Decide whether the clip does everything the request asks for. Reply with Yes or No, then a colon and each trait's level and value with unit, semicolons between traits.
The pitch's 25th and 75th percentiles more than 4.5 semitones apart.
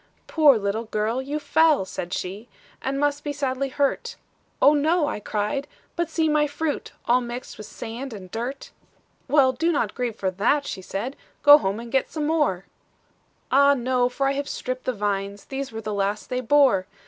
Yes: average, 5.2 semitones